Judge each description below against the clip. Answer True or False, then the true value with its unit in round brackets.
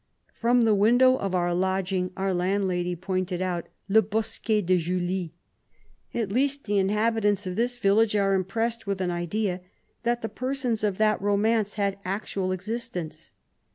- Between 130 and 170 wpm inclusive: True (160 wpm)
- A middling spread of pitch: True (3.2 semitones)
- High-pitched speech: True (200 Hz)